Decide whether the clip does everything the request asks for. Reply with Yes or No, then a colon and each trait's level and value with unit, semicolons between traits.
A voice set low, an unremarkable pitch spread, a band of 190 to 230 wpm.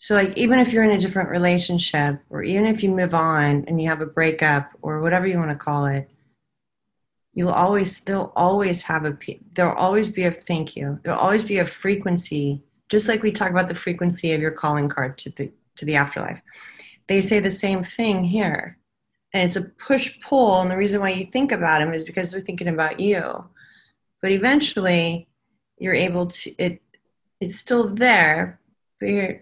No: medium, 180 Hz; average, 3.8 semitones; average, 195 wpm